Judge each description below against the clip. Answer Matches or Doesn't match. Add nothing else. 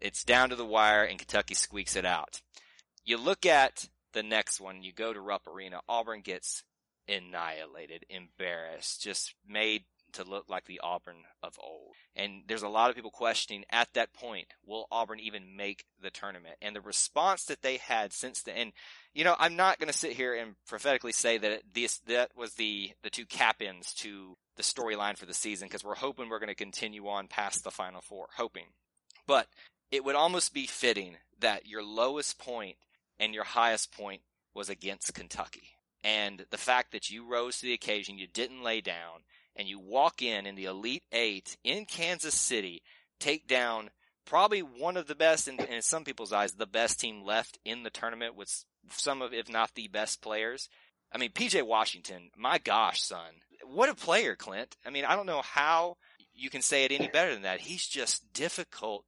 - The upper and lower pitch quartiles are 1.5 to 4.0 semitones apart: Doesn't match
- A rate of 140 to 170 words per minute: Doesn't match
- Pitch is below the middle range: Matches